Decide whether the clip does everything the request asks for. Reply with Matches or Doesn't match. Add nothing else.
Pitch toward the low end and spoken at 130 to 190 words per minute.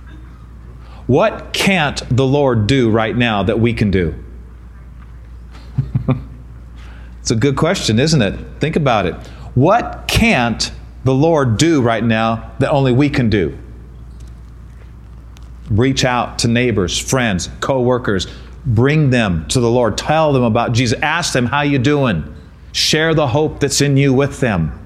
Matches